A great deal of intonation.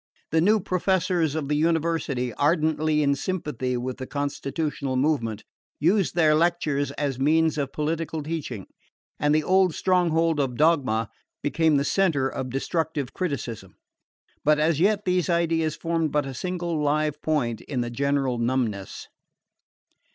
No: average, 3.3 semitones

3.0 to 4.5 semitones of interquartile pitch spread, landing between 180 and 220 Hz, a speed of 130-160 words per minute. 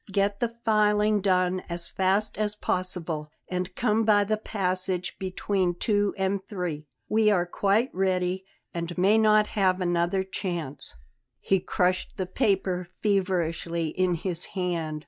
No: narrow, 2.5 semitones; medium, 185 Hz; average, 140 wpm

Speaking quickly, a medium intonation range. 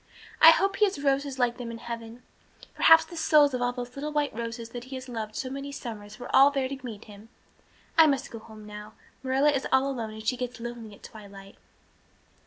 Yes: fast, 220 wpm; average, 3.5 semitones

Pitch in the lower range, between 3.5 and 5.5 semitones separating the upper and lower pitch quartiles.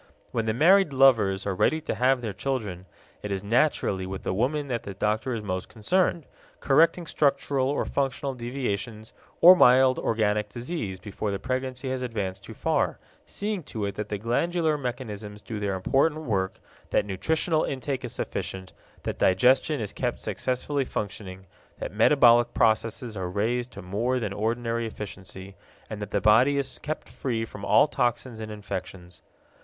Yes: low, 115 Hz; average, 4.7 semitones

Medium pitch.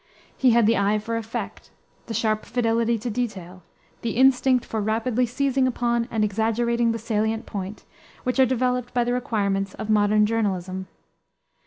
No: high, 230 Hz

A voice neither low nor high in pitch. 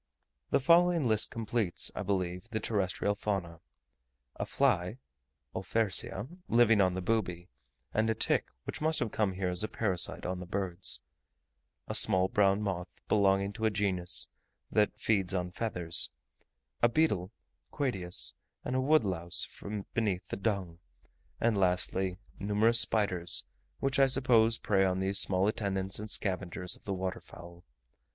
No: low, 100 Hz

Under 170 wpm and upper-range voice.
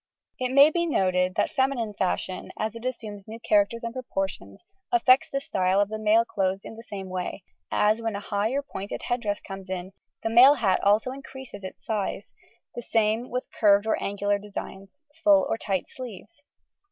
No: average, 190 wpm; high, 215 Hz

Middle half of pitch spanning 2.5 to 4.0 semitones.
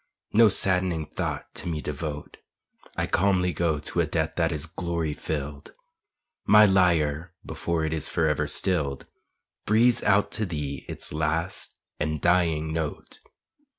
Yes: average, 3.0 semitones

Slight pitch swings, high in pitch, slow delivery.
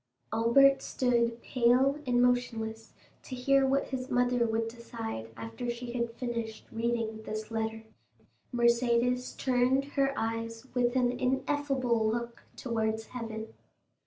Yes: narrow, 1.9 semitones; high, 235 Hz; slow, 125 wpm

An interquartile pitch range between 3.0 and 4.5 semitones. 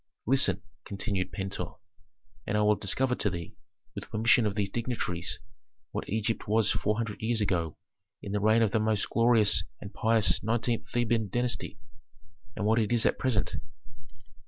No: narrow, 2.4 semitones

